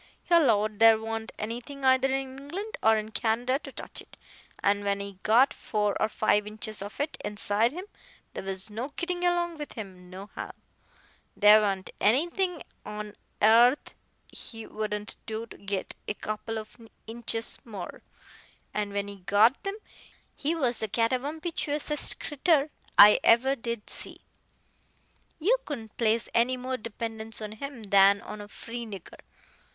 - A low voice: No, high, 225 Hz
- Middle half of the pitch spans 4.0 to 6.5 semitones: Yes, average, 4.3 semitones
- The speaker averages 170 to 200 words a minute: No, average, 155 wpm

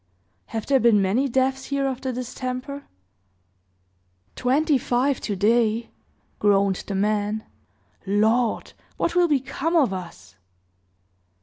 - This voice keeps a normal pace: No, slow, 115 wpm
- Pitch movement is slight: No, average, 4.5 semitones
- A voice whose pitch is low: No, high, 245 Hz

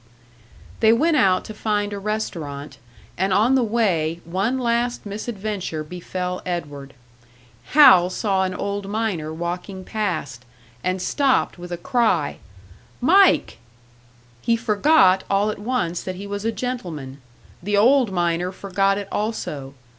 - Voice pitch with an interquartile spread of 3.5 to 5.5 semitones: Yes, average, 4.1 semitones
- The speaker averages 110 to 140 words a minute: Yes, slow, 135 wpm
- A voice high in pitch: Yes, high, 195 Hz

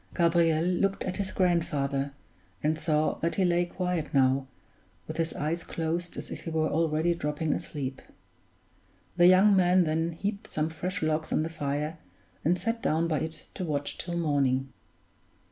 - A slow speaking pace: No, average, 165 wpm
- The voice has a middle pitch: Yes, medium, 165 Hz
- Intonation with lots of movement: No, narrow, 2.5 semitones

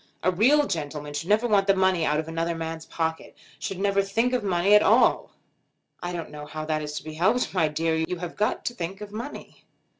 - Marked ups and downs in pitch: No, average, 4.0 semitones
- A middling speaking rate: No, fast, 230 wpm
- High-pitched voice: No, medium, 175 Hz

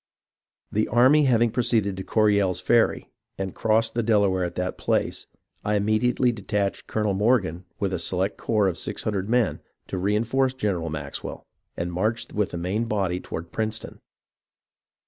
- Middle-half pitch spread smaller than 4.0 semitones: Yes, average, 3.4 semitones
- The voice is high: No, low, 105 Hz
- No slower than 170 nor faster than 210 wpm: No, average, 155 wpm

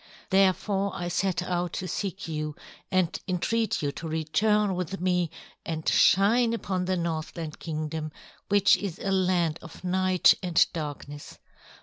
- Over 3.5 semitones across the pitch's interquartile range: No, average, 3.2 semitones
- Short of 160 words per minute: Yes, average, 140 wpm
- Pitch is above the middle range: No, medium, 180 Hz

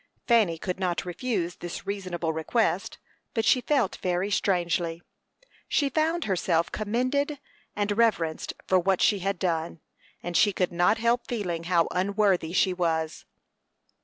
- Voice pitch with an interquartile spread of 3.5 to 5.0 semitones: Yes, average, 4.3 semitones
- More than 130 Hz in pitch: Yes, high, 190 Hz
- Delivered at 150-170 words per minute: No, average, 140 wpm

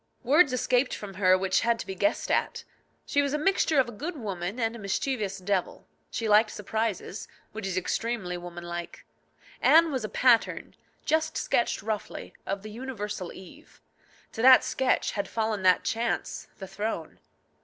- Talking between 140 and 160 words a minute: No, average, 170 wpm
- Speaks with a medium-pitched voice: No, high, 220 Hz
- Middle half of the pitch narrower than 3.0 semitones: No, average, 4.9 semitones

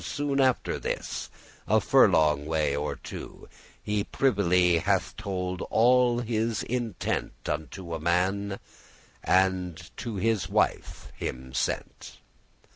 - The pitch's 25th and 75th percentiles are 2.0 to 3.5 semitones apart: No, average, 5.2 semitones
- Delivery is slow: Yes, slow, 115 wpm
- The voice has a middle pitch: No, very low, 95 Hz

